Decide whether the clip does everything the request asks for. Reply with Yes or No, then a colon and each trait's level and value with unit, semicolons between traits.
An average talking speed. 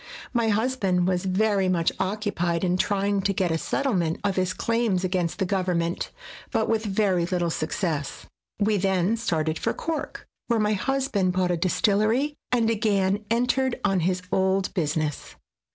Yes: average, 160 wpm